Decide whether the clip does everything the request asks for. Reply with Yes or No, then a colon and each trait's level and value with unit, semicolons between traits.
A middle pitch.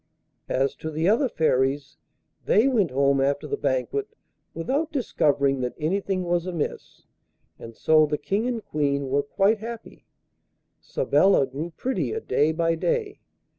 Yes: medium, 165 Hz